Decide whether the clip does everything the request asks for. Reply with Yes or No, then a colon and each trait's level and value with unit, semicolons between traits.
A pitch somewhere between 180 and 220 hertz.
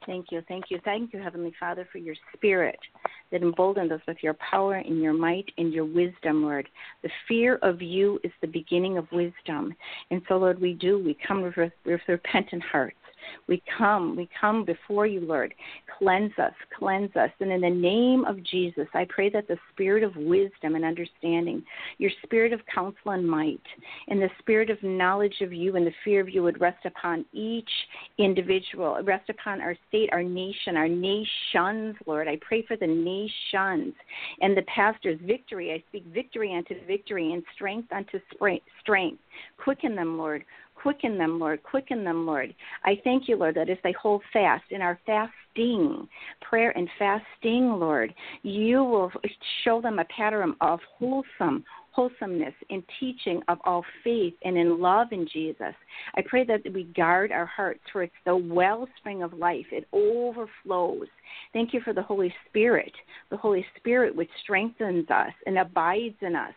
Yes: high, 190 Hz